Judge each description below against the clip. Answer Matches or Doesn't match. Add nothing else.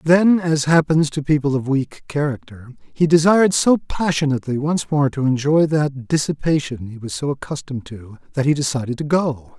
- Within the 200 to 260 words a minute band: Doesn't match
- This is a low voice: Doesn't match